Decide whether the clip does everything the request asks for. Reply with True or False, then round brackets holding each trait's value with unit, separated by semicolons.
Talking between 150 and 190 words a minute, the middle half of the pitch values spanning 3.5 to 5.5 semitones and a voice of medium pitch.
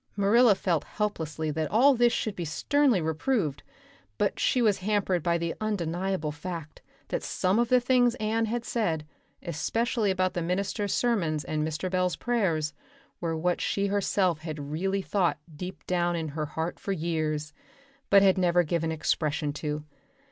True (160 wpm; 4.7 semitones; 180 Hz)